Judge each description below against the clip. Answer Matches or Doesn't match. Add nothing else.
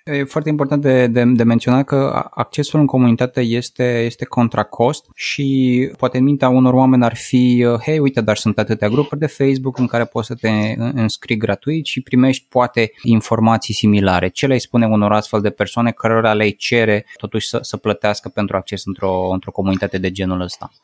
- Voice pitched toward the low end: Matches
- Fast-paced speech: Matches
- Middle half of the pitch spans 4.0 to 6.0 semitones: Doesn't match